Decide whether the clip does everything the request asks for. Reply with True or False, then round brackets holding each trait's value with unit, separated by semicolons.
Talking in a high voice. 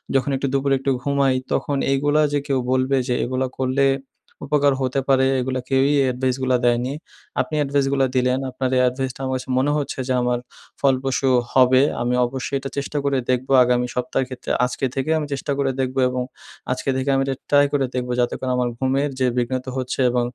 False (130 Hz)